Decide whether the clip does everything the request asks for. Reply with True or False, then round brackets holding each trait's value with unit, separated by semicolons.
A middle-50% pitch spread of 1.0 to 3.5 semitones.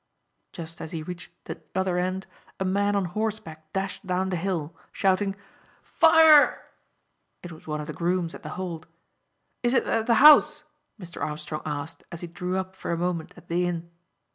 True (2.7 semitones)